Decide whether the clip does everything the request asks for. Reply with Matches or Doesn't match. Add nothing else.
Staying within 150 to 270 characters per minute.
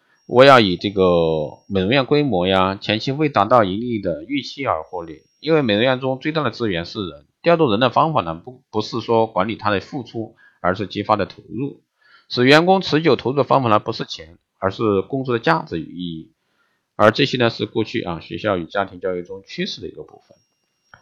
Doesn't match